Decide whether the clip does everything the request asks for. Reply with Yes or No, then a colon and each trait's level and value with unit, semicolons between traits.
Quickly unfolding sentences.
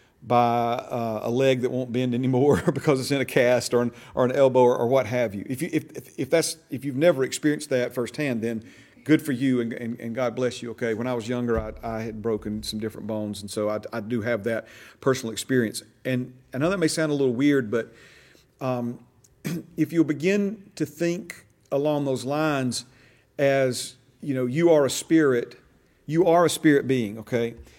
Yes: fast, 210 wpm